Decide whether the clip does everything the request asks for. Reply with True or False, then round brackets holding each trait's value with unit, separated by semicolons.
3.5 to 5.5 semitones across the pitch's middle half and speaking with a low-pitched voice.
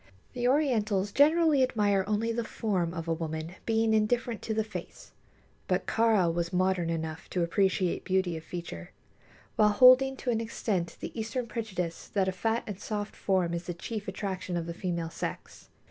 False (4.7 semitones; 200 Hz)